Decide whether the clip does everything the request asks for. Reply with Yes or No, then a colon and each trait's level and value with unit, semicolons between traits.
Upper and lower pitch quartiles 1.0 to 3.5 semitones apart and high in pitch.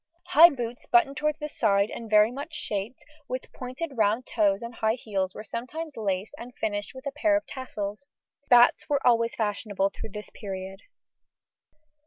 No: average, 4.8 semitones; high, 230 Hz